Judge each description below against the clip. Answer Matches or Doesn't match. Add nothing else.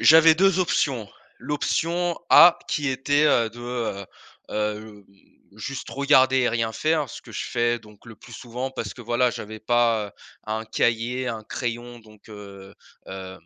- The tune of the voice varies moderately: Matches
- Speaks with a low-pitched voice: Matches